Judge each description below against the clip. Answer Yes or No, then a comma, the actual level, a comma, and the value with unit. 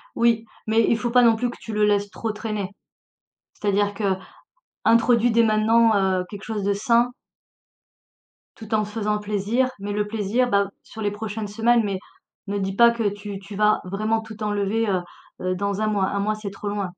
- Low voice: No, high, 210 Hz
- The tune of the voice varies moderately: No, narrow, 1.9 semitones